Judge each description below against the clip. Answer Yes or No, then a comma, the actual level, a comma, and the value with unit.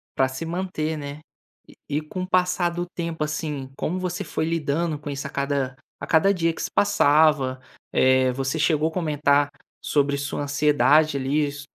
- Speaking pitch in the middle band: Yes, medium, 150 Hz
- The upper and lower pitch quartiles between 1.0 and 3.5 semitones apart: Yes, average, 2.8 semitones